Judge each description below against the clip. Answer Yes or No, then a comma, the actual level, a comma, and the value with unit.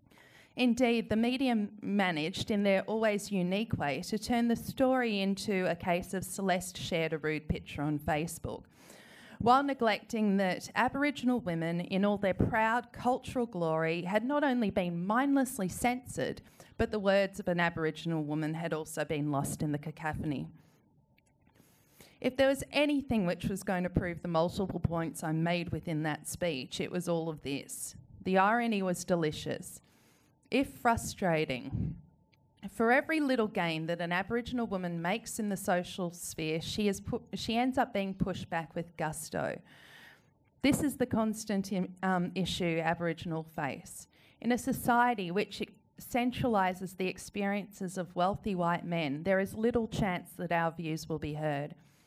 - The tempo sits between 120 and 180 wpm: Yes, average, 160 wpm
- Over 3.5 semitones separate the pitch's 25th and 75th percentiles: Yes, average, 5.1 semitones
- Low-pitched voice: No, high, 190 Hz